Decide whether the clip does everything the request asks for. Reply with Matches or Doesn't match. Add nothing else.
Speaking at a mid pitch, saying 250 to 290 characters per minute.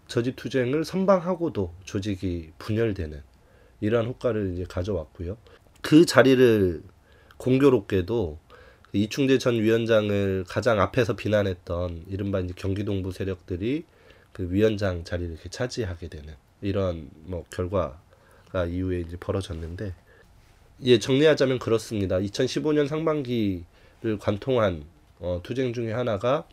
Doesn't match